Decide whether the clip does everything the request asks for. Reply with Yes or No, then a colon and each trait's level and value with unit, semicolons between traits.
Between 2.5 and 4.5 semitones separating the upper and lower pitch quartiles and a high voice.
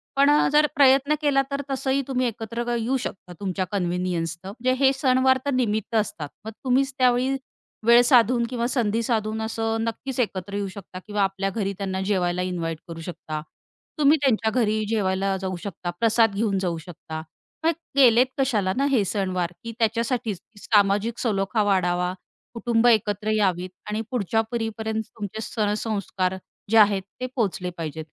Yes: average, 4.2 semitones; high, 215 Hz